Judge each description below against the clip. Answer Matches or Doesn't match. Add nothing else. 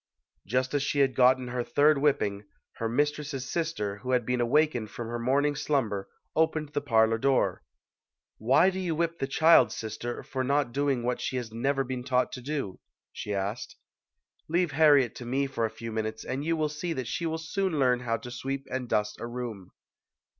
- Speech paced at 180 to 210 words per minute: Matches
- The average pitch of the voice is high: Doesn't match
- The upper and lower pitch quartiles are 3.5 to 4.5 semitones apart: Matches